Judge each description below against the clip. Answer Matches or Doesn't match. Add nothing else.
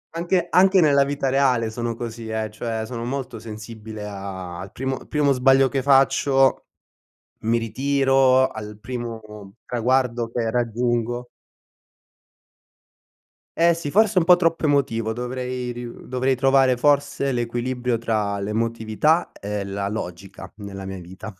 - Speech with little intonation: Doesn't match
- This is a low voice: Matches